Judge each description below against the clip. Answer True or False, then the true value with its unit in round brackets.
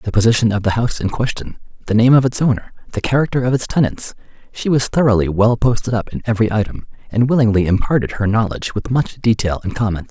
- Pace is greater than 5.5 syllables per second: True (6.5 syllables/s)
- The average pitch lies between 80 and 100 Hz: False (110 Hz)